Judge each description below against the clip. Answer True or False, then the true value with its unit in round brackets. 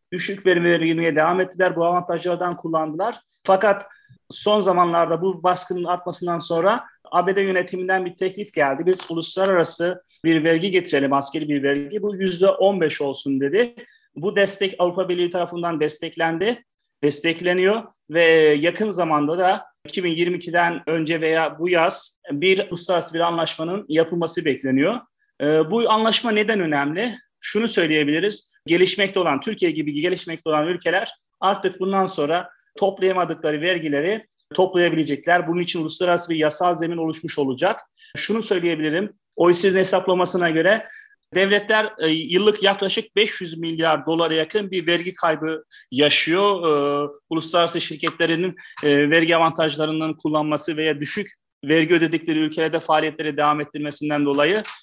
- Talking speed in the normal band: True (120 wpm)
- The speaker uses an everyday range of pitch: True (3.0 semitones)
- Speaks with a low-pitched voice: False (175 Hz)